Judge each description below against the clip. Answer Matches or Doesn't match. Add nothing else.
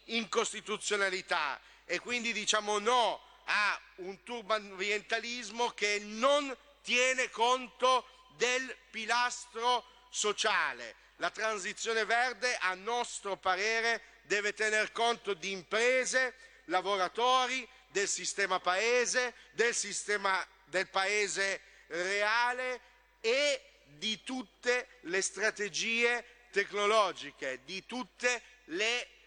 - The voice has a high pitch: Matches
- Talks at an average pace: Doesn't match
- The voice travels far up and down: Doesn't match